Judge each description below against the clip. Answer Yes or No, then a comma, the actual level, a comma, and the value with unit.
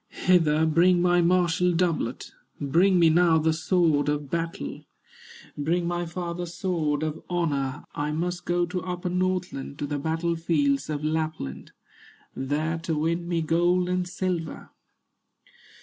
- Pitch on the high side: No, medium, 165 Hz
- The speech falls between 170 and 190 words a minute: No, average, 140 wpm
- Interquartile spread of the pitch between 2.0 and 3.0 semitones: Yes, narrow, 2.5 semitones